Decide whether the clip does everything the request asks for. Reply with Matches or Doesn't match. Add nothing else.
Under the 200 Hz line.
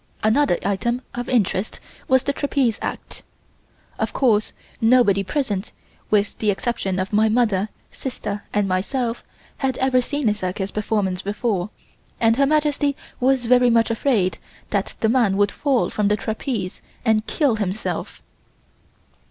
Doesn't match